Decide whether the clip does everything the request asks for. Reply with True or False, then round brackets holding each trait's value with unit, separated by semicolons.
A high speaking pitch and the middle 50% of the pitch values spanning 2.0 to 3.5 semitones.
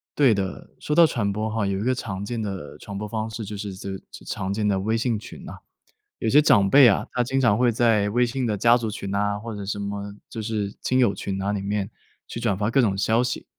False (105 Hz; 2.8 semitones)